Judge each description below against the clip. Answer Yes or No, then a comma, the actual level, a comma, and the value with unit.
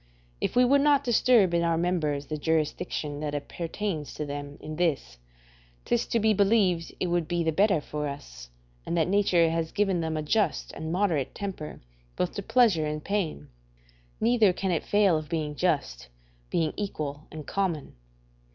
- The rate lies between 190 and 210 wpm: No, average, 175 wpm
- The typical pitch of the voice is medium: Yes, medium, 170 Hz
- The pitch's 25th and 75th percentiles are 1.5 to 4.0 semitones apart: No, average, 4.7 semitones